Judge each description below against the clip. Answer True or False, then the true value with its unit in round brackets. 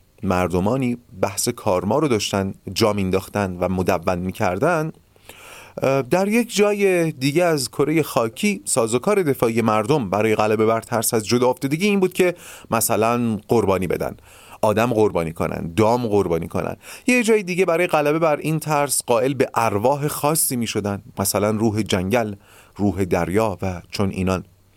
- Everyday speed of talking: True (145 wpm)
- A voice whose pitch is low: True (115 Hz)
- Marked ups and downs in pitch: True (7.0 semitones)